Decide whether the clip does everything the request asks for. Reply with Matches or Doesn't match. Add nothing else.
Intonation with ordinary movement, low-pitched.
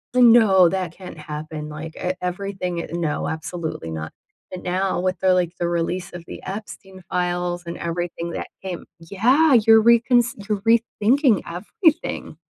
Doesn't match